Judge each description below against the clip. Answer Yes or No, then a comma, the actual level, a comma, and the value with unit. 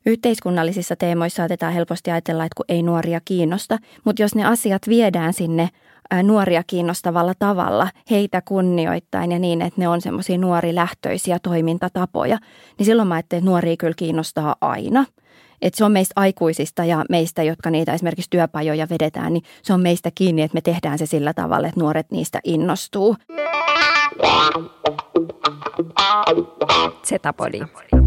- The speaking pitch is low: No, medium, 175 Hz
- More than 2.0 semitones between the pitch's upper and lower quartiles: Yes, narrow, 2.4 semitones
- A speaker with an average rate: Yes, average, 145 wpm